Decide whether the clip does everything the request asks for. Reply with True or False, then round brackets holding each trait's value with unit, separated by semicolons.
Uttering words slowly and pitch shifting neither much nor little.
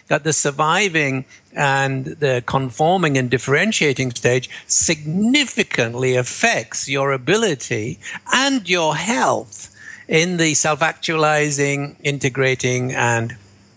True (95 wpm; 3.6 semitones)